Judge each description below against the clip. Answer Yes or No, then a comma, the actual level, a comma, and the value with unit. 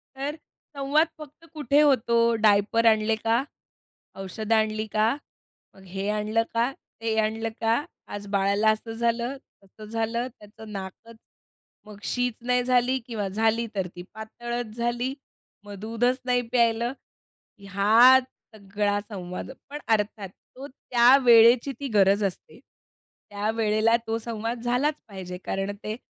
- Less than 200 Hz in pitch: No, high, 225 Hz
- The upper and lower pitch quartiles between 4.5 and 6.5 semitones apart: No, average, 2.7 semitones